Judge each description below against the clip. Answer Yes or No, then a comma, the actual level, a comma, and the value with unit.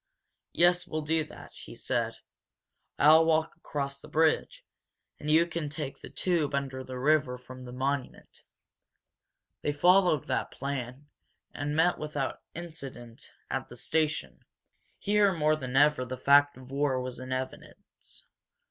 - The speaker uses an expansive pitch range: No, average, 3.4 semitones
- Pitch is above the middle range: No, medium, 145 Hz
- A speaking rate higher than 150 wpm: No, average, 145 wpm